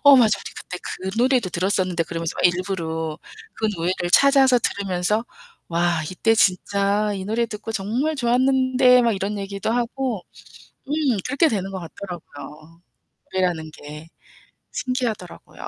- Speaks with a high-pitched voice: Yes, high, 200 Hz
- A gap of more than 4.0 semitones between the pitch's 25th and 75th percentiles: Yes, wide, 5.4 semitones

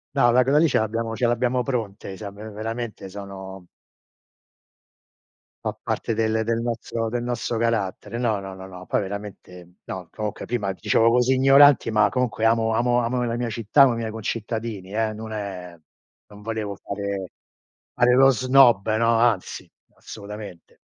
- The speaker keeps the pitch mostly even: No, average, 3.0 semitones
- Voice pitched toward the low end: Yes, low, 110 Hz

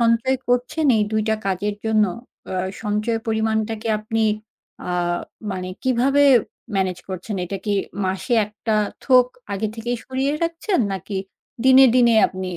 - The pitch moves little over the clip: No, average, 3.3 semitones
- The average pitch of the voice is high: Yes, high, 220 Hz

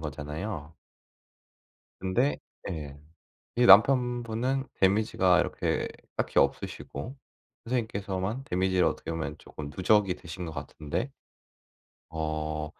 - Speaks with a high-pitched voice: No, very low, 95 Hz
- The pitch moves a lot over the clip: Yes, wide, 6.6 semitones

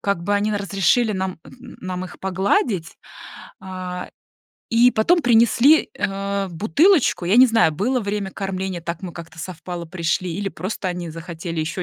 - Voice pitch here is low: No, high, 190 Hz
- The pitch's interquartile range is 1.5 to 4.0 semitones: Yes, average, 3.5 semitones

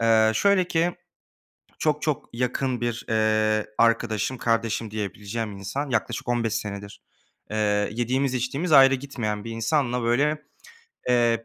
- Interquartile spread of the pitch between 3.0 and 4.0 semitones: Yes, average, 3.6 semitones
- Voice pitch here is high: No, low, 115 Hz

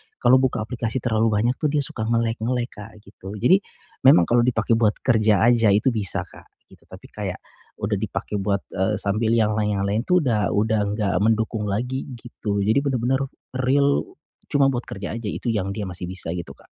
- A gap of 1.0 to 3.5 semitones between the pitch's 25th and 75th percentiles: Yes, average, 3.1 semitones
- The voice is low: Yes, low, 110 Hz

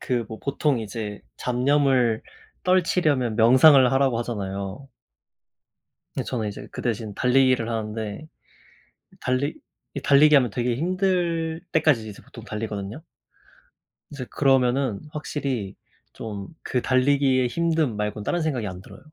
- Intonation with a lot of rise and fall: No, average, 4.5 semitones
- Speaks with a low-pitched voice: Yes, low, 125 Hz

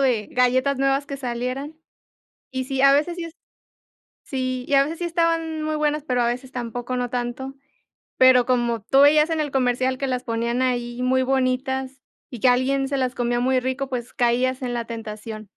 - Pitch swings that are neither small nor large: No, narrow, 2.0 semitones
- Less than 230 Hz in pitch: No, very high, 255 Hz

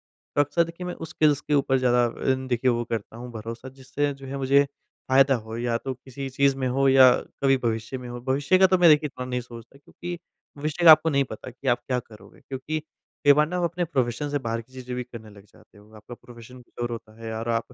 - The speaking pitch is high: No, low, 130 Hz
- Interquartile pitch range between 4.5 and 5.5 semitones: No, average, 3.1 semitones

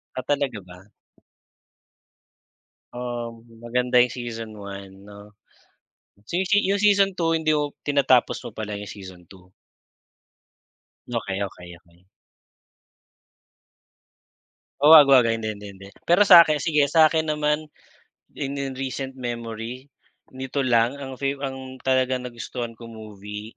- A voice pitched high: No, low, 125 Hz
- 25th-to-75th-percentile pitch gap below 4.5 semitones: No, average, 4.9 semitones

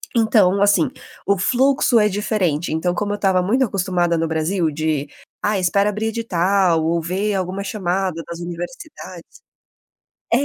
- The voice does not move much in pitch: No, average, 3.4 semitones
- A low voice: No, medium, 185 Hz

